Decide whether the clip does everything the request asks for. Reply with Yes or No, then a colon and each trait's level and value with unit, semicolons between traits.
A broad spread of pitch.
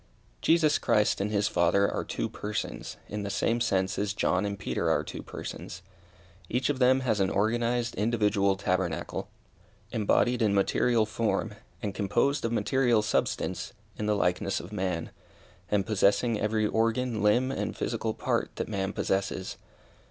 No: average, 2.9 semitones